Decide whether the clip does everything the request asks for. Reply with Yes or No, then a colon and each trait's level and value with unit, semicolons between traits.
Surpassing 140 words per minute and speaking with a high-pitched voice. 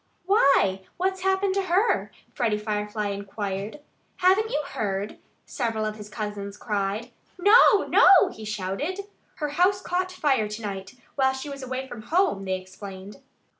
Yes: average, 150 wpm; high, 225 Hz